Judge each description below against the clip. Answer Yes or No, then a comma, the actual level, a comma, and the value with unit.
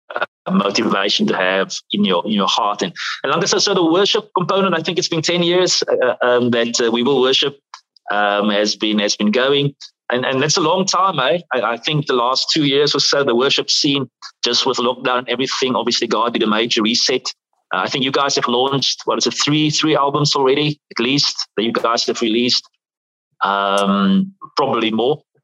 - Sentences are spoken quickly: Yes, fast, 215 wpm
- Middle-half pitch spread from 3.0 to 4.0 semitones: No, wide, 5.4 semitones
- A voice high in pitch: No, low, 135 Hz